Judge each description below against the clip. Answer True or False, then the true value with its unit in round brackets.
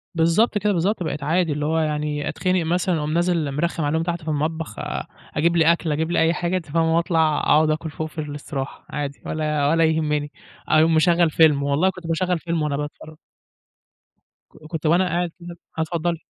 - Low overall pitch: False (160 Hz)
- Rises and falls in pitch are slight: True (2.1 semitones)